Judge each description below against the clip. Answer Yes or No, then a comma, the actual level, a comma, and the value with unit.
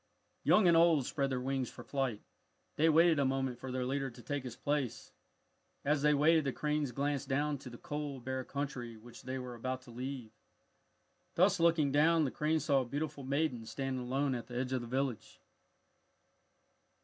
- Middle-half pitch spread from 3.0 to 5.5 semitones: No, narrow, 2.6 semitones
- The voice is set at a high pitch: No, low, 135 Hz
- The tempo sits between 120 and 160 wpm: No, average, 190 wpm